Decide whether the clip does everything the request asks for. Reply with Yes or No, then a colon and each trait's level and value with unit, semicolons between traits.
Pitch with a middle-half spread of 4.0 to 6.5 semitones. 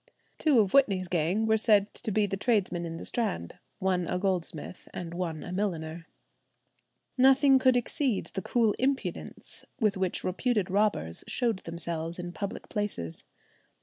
Yes: average, 4.4 semitones